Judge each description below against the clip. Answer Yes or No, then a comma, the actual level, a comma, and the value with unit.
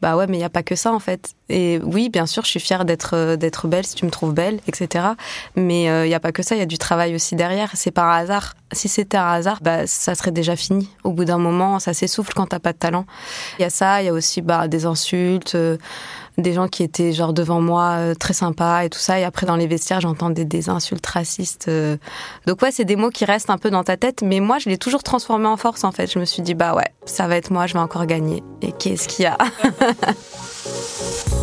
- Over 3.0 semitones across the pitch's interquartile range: No, narrow, 2.5 semitones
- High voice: No, medium, 180 Hz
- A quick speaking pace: Yes, fast, 260 wpm